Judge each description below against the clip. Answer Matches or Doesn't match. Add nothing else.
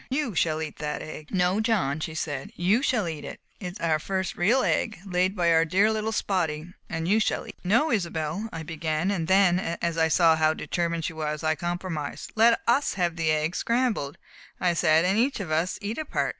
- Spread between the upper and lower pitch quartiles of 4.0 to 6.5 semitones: Matches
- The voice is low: Doesn't match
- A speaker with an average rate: Doesn't match